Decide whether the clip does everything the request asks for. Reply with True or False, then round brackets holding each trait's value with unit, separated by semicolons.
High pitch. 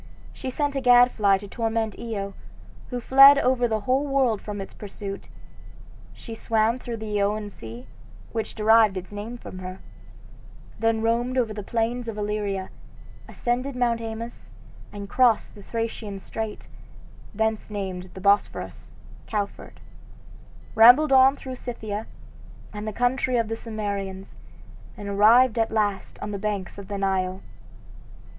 True (220 Hz)